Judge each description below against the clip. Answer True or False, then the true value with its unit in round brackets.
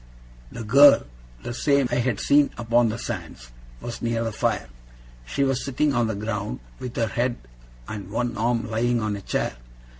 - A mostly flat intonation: True (2.3 semitones)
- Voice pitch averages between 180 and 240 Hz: False (115 Hz)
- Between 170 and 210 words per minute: True (180 wpm)